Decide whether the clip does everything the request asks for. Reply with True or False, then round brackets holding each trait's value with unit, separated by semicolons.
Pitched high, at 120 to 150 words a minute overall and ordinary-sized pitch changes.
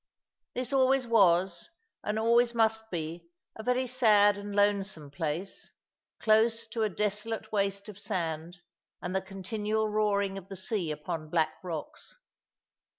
True (205 Hz; 140 wpm; 3.9 semitones)